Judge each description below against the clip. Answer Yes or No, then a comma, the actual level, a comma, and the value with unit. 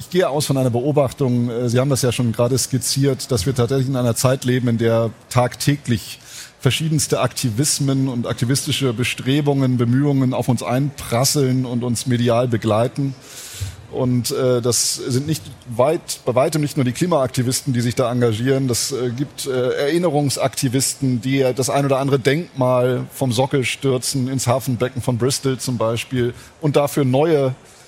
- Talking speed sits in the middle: Yes, average, 155 wpm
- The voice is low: Yes, low, 130 Hz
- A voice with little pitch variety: Yes, narrow, 2.0 semitones